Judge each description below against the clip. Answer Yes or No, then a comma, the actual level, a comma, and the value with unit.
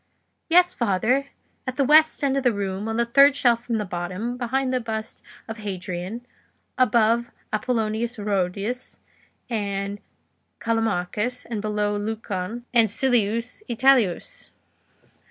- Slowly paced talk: Yes, slow, 125 wpm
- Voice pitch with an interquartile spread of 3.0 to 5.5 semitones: Yes, average, 3.3 semitones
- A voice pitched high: Yes, high, 225 Hz